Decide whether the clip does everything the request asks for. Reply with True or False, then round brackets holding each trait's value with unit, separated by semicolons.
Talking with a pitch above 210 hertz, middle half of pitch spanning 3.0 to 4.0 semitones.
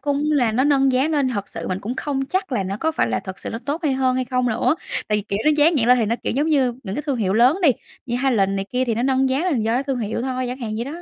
True (255 Hz; 3.7 semitones)